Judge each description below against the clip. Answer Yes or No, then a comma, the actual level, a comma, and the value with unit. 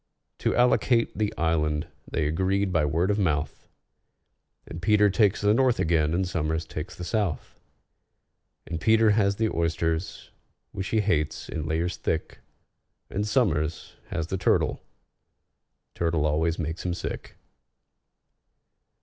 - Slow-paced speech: Yes, slow, 130 wpm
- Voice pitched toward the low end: Yes, very low, 85 Hz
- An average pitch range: Yes, average, 4.3 semitones